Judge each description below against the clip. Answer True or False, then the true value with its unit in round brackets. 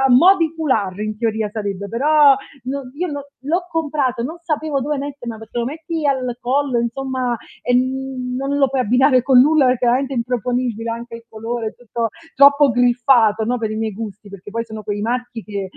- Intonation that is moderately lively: True (3.6 semitones)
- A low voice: False (250 Hz)